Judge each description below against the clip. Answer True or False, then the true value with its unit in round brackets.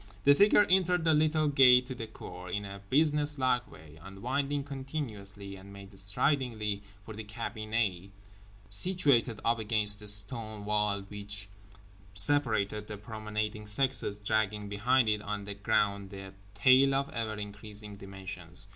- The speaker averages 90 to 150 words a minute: True (140 wpm)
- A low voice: True (105 Hz)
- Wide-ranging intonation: False (4.2 semitones)